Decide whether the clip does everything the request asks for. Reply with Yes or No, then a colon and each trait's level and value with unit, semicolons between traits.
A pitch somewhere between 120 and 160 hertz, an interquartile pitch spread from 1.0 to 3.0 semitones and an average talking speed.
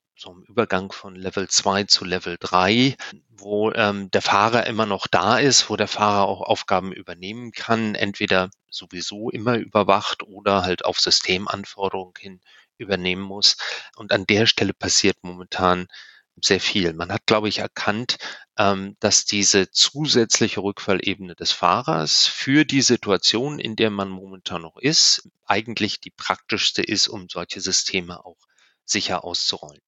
No: low, 100 Hz; narrow, 2.4 semitones; average, 150 wpm